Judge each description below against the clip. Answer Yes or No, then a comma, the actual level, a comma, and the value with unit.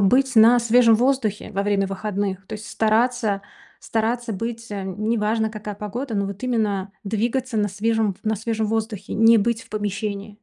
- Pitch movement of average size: No, narrow, 2.2 semitones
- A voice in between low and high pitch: No, high, 215 Hz